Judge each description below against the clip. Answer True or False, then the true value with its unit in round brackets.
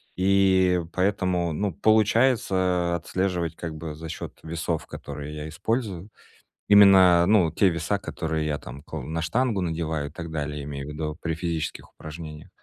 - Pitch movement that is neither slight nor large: True (3.3 semitones)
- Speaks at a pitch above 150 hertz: False (85 Hz)